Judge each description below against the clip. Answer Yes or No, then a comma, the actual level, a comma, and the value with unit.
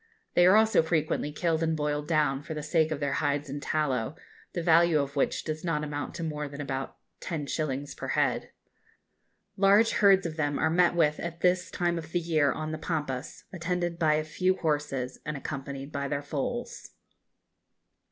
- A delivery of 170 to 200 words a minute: Yes, average, 185 wpm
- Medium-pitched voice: Yes, medium, 155 Hz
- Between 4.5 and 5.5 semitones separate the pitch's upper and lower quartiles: No, average, 2.7 semitones